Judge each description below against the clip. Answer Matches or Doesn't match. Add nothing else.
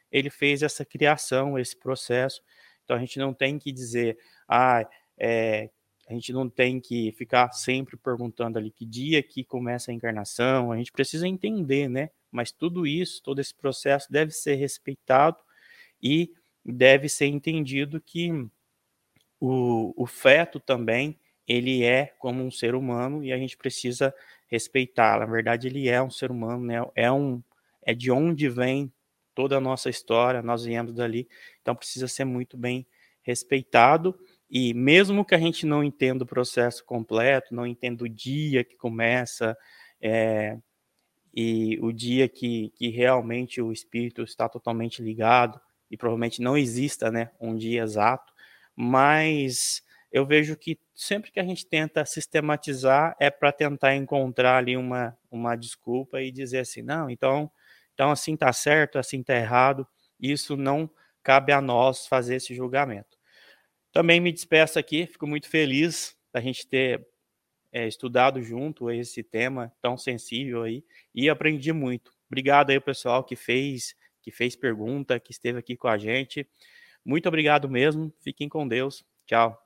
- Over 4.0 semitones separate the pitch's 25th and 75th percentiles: Doesn't match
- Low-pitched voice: Matches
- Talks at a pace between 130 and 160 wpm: Matches